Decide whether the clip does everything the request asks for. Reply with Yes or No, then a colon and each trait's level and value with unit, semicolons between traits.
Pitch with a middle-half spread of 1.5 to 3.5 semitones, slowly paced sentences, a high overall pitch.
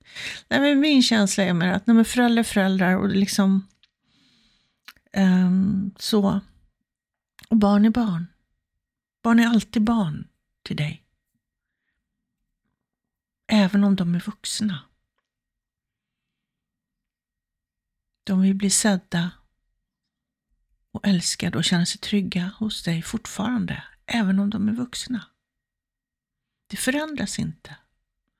Yes: average, 2.9 semitones; slow, 105 wpm; high, 200 Hz